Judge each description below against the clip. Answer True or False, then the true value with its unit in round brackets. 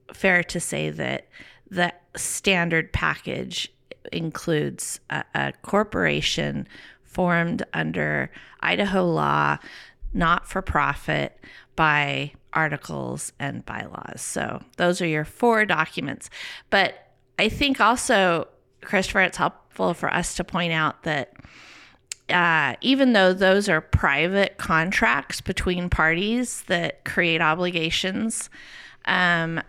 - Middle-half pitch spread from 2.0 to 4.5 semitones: True (3.4 semitones)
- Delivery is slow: True (110 wpm)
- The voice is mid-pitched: True (175 Hz)